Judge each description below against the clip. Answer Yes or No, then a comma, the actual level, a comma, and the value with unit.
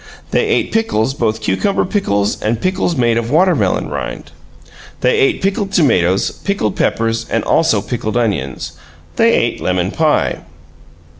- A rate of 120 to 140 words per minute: Yes, slow, 135 wpm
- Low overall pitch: Yes, low, 120 Hz